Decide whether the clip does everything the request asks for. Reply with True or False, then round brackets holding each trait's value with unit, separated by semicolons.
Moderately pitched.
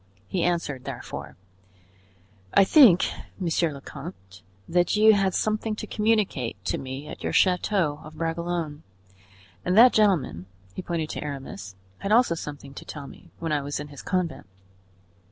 True (165 Hz)